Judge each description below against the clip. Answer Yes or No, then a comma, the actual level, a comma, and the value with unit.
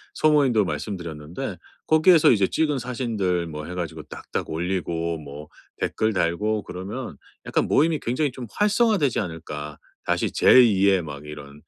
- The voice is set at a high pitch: No, very low, 95 Hz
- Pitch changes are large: Yes, wide, 7.8 semitones